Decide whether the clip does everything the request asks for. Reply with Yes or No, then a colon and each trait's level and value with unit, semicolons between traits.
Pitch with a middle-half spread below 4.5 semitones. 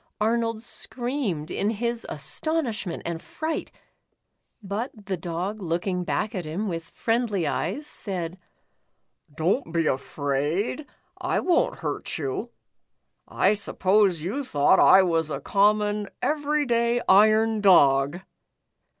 No: wide, 5.6 semitones